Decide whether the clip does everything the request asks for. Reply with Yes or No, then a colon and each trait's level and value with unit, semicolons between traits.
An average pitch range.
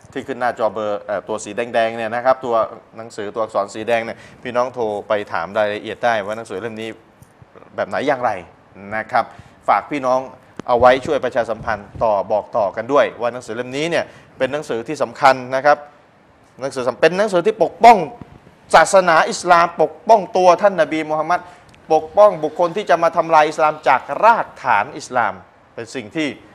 No: wide, 6.0 semitones